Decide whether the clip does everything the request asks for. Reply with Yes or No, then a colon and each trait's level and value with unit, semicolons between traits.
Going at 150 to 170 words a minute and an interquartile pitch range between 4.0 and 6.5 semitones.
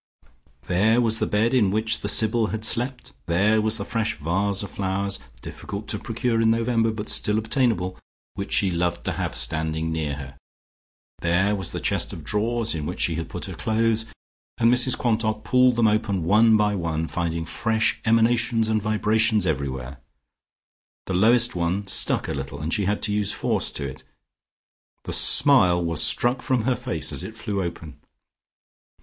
No: average, 180 wpm; average, 4.5 semitones